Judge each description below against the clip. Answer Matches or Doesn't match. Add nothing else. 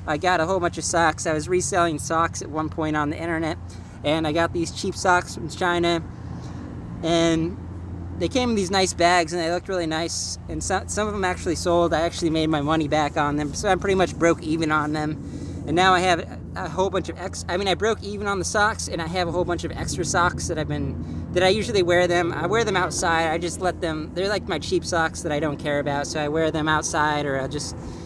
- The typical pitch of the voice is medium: Matches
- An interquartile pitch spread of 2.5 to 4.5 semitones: Matches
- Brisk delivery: Matches